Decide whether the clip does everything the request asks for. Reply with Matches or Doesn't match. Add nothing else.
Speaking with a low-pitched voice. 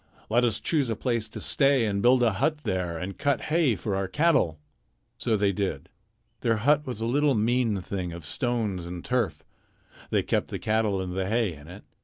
Matches